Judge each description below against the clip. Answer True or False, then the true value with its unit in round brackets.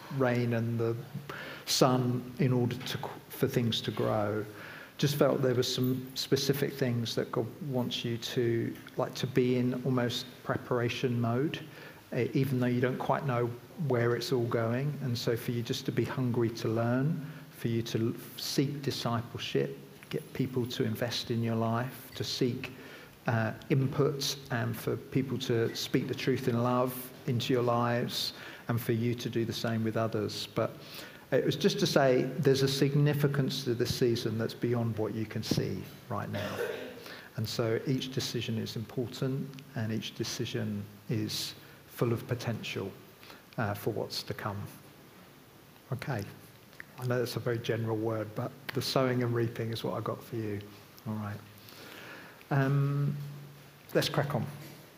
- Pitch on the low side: True (125 Hz)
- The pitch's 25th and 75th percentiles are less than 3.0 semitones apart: True (2.6 semitones)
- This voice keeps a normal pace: True (165 wpm)